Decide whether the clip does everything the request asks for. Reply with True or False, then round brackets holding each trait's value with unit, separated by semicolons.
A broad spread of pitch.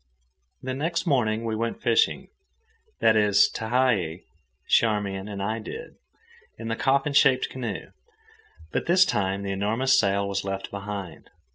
False (4.7 semitones)